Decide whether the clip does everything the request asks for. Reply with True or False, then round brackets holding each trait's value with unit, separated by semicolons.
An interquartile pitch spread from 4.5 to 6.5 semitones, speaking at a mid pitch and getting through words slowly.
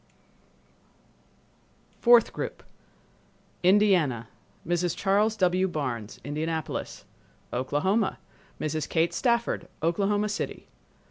True (5.1 semitones; 175 Hz; 65 wpm)